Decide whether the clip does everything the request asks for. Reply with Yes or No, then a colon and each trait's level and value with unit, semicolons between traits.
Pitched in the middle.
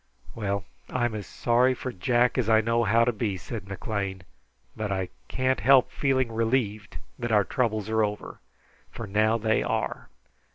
No: low, 110 Hz